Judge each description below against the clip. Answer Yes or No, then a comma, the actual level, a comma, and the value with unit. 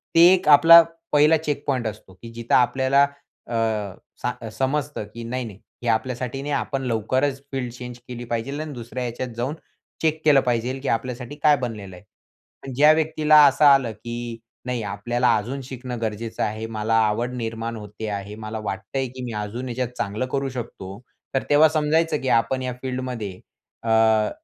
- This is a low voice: Yes, low, 125 Hz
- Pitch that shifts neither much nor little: Yes, average, 3.4 semitones